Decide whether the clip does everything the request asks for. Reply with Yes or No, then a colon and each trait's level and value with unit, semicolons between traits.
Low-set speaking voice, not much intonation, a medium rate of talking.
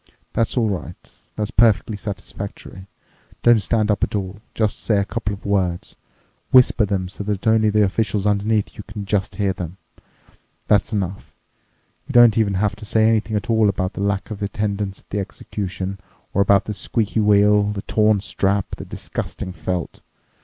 Yes: low, 105 Hz; narrow, 1.6 semitones; average, 175 wpm